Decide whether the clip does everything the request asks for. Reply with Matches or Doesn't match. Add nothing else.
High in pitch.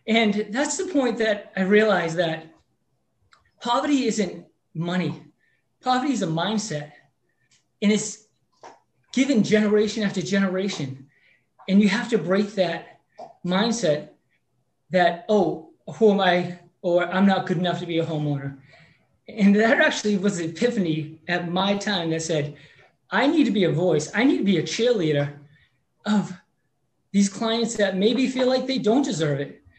Matches